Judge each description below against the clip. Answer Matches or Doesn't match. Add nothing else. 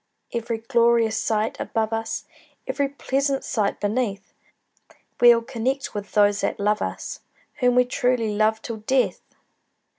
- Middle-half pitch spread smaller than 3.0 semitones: Matches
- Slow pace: Matches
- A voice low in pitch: Doesn't match